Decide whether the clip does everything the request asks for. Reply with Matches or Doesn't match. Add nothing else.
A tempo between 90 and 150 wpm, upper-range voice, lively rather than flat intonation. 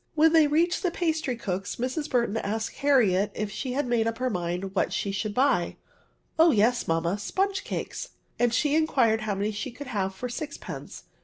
Doesn't match